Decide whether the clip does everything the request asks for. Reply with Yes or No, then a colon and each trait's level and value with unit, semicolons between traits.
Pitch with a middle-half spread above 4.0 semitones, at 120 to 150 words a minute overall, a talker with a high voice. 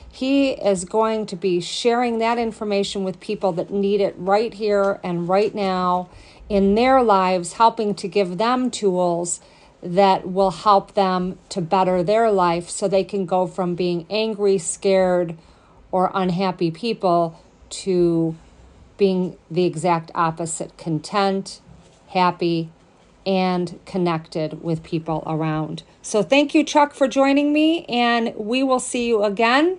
No: average, 3.6 semitones; average, 140 wpm; high, 195 Hz